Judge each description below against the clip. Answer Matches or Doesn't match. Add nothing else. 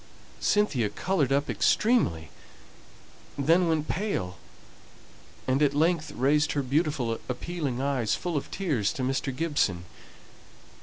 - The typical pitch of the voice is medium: Matches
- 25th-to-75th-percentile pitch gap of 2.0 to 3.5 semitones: Doesn't match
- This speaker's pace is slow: Matches